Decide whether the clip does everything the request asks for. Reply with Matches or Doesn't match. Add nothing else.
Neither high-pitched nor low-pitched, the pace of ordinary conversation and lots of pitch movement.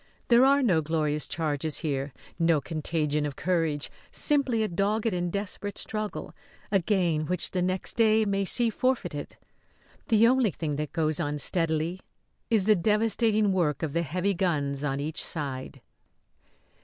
Matches